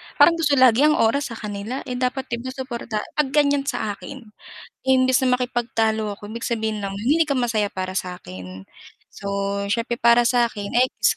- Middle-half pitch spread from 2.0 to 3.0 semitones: No, average, 3.6 semitones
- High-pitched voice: Yes, high, 235 Hz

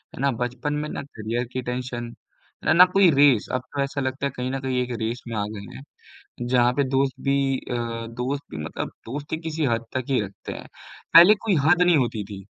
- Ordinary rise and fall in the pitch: Yes, average, 3.1 semitones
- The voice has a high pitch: No, low, 130 Hz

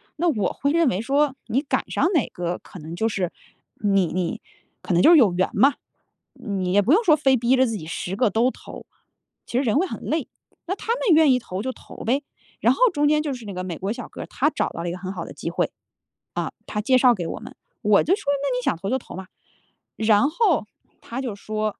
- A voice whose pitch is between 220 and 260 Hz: Yes, high, 235 Hz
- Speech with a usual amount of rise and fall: No, wide, 6.5 semitones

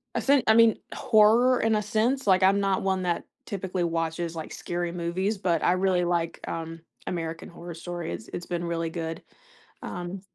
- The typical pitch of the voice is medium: Yes, medium, 180 Hz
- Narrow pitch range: No, average, 3.0 semitones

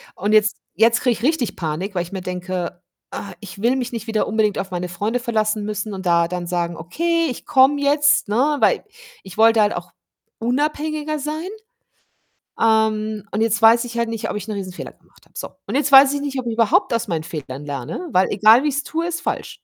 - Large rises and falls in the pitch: Yes, wide, 5.8 semitones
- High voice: Yes, high, 220 Hz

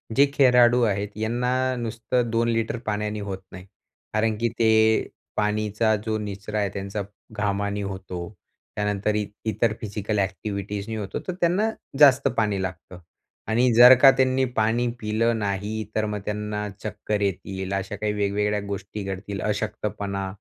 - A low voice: Yes, low, 105 Hz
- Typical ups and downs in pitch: No, narrow, 2.2 semitones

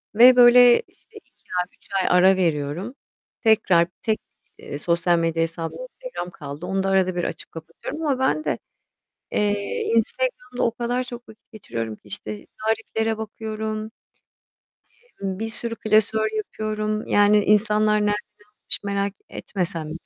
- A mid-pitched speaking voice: No, high, 210 Hz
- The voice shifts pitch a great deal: No, average, 4.1 semitones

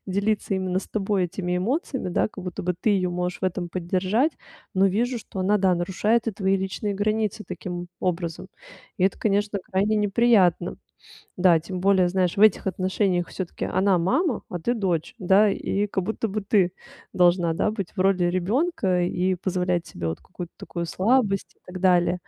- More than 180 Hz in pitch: Yes, high, 190 Hz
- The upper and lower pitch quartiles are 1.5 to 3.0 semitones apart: Yes, narrow, 2.5 semitones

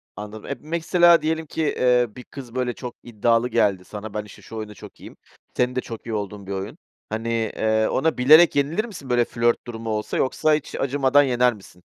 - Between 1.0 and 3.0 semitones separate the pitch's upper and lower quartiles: No, average, 4.4 semitones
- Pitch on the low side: Yes, low, 120 Hz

